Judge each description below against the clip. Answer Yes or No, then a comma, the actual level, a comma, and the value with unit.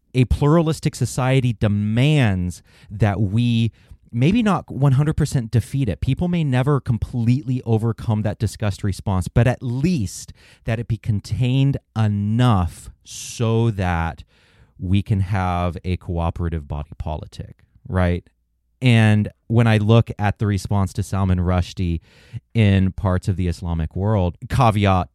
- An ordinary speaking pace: No, slow, 130 wpm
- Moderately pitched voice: No, low, 110 Hz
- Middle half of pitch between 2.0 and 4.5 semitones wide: No, average, 4.9 semitones